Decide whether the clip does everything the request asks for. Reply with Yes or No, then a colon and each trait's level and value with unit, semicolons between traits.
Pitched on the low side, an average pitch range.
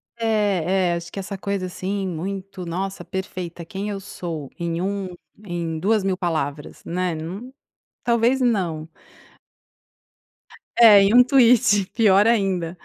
No: high, 190 Hz; average, 3.0 semitones